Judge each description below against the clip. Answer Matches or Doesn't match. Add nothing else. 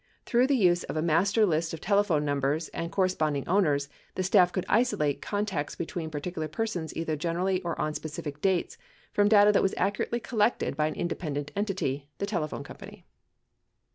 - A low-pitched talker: Doesn't match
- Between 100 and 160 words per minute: Doesn't match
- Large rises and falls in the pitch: Doesn't match